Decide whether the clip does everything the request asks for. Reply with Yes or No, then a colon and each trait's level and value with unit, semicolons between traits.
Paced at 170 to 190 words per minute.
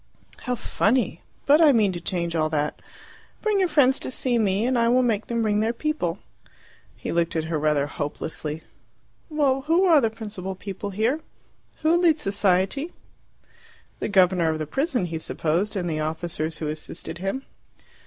Yes: average, 175 wpm